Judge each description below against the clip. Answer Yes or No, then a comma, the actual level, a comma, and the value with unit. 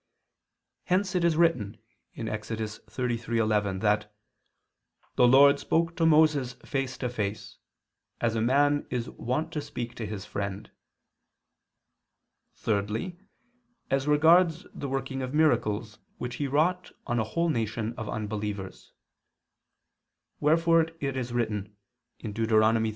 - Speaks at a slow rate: Yes, slow, 120 wpm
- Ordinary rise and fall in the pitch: No, wide, 5.7 semitones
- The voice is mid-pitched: No, low, 125 Hz